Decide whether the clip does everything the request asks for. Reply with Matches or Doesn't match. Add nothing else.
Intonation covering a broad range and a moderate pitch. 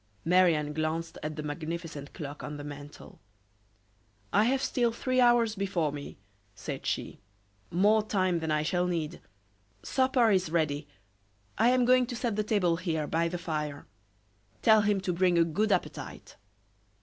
Matches